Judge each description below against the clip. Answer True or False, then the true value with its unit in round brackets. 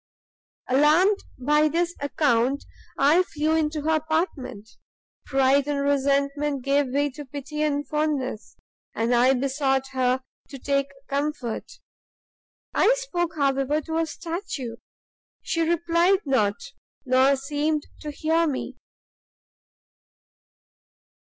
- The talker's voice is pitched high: True (285 Hz)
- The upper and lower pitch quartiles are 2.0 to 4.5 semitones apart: True (2.8 semitones)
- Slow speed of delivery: True (110 wpm)